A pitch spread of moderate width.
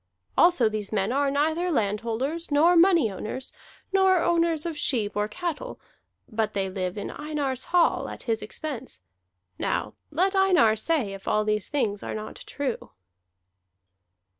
No: wide, 7.8 semitones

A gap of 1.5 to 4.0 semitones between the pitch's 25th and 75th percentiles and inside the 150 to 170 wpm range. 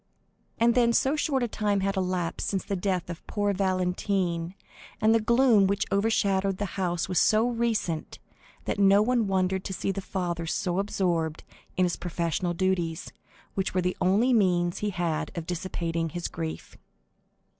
Yes: average, 2.8 semitones; average, 165 wpm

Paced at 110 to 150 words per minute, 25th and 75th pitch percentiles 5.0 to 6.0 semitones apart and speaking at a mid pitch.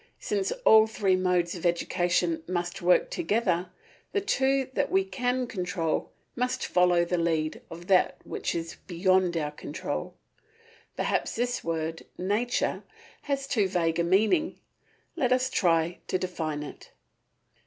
Yes: average, 140 wpm; wide, 5.5 semitones; medium, 180 Hz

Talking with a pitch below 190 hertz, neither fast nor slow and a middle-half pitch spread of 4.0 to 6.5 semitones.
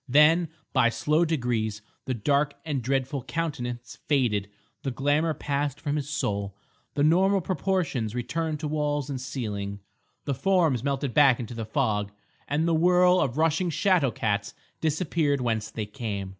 Yes: medium, 140 Hz; average, 155 wpm; average, 4.9 semitones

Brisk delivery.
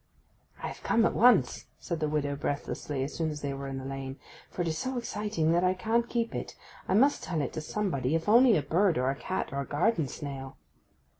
Yes: fast, 235 wpm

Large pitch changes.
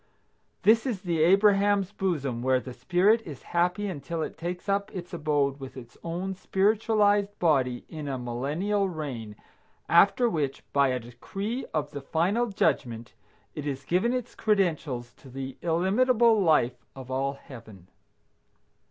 Yes: wide, 6.8 semitones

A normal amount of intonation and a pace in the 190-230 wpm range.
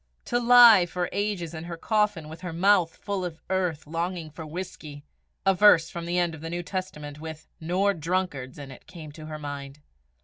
Yes: average, 3.3 semitones; average, 200 wpm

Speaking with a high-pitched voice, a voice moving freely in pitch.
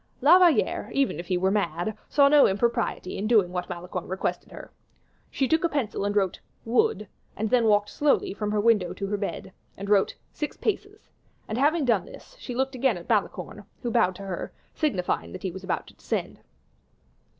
Yes: high, 210 Hz; wide, 5.9 semitones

